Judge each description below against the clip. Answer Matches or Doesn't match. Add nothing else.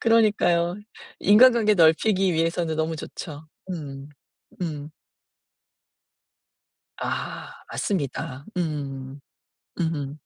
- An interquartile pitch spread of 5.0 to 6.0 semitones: Doesn't match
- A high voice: Doesn't match